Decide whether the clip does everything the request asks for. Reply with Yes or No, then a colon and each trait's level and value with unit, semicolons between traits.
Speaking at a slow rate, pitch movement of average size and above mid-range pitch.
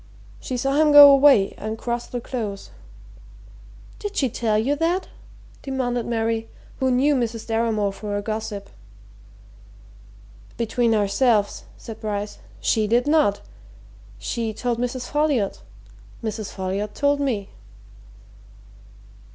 Yes: slow, 120 wpm; average, 3.8 semitones; high, 235 Hz